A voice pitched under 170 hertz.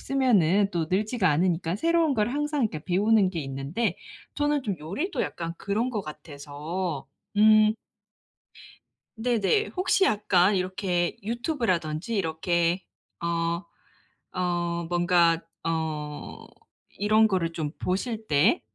No: medium, 185 Hz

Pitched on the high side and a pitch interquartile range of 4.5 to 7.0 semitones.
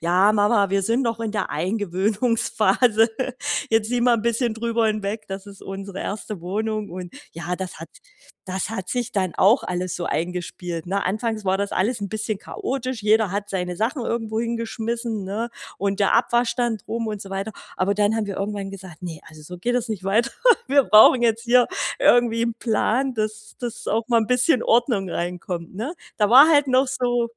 No: high, 215 Hz; average, 3.3 semitones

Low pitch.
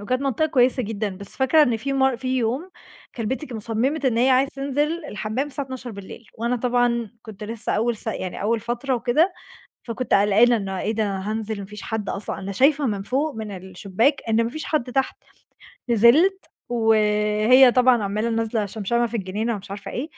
No: high, 235 Hz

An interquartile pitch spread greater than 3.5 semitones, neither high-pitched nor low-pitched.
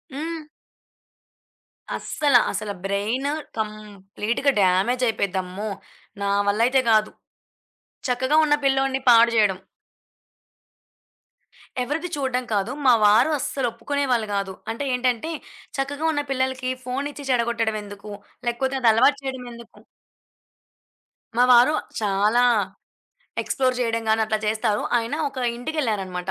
No: average, 3.9 semitones; high, 235 Hz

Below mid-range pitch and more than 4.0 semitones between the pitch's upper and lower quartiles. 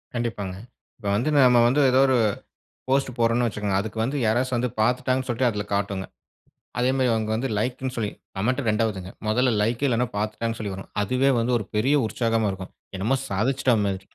No: low, 115 Hz; average, 3.3 semitones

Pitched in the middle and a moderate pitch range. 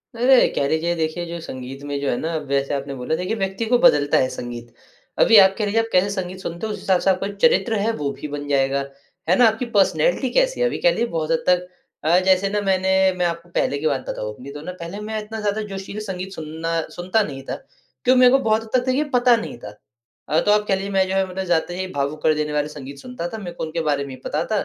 No: medium, 180 Hz; wide, 5.9 semitones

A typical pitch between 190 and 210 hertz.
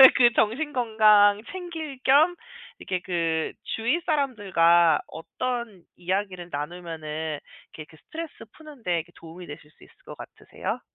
Yes: high, 200 Hz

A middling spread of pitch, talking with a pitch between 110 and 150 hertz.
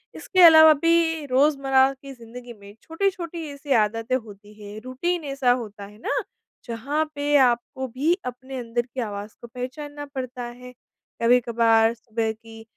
No: average, 4.1 semitones; very high, 250 Hz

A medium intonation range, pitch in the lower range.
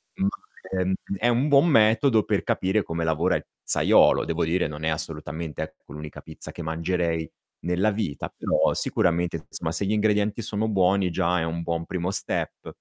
Yes: average, 4.0 semitones; very low, 90 Hz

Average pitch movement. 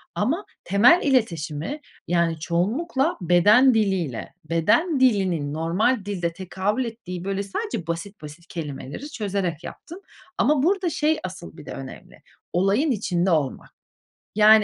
No: wide, 7.0 semitones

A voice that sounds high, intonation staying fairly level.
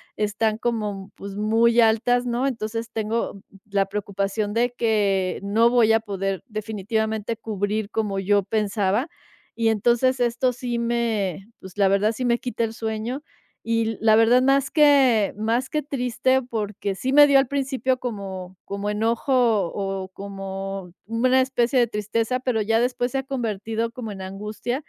No: high, 225 Hz; average, 3.2 semitones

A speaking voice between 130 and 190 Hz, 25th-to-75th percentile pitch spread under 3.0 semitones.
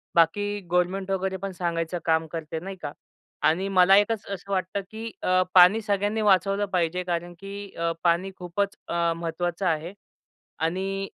Yes: medium, 185 Hz; narrow, 2.6 semitones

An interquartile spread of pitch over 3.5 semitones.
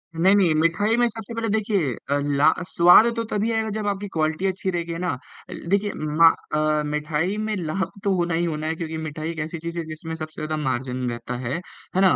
Yes: average, 4.4 semitones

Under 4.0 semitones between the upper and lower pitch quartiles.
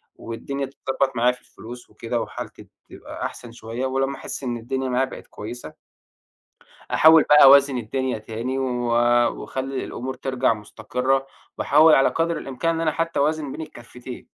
Yes: narrow, 2.4 semitones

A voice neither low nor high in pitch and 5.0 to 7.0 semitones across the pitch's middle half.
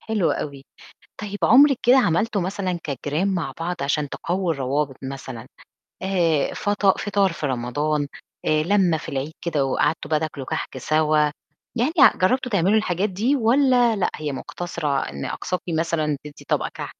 Yes: medium, 170 Hz; wide, 5.6 semitones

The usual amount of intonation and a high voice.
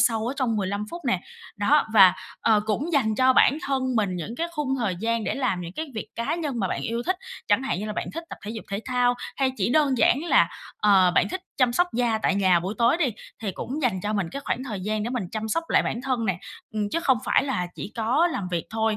Yes: average, 4.5 semitones; high, 230 Hz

